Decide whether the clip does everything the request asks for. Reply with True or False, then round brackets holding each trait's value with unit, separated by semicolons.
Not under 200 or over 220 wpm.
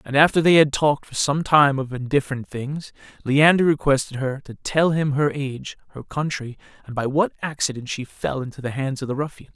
True (205 wpm)